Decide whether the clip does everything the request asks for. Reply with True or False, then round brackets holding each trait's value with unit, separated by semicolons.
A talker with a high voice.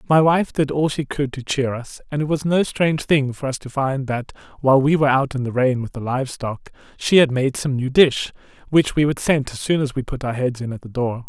False (135 Hz)